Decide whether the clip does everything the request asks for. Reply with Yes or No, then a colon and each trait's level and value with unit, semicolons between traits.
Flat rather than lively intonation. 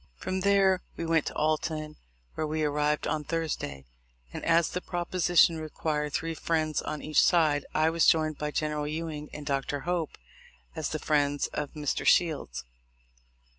Yes: narrow, 1.8 semitones